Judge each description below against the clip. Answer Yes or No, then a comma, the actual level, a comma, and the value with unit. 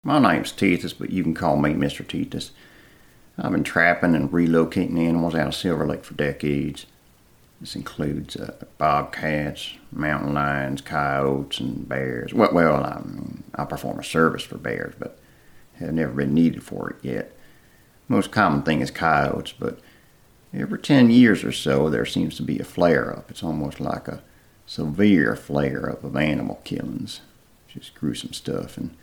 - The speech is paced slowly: No, average, 155 wpm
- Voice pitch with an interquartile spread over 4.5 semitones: No, average, 2.8 semitones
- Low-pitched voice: Yes, very low, 75 Hz